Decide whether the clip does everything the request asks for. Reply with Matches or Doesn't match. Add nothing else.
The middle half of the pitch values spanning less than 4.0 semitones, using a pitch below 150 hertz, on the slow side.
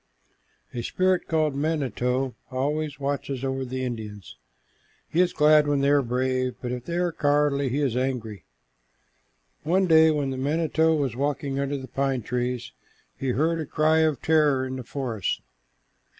Doesn't match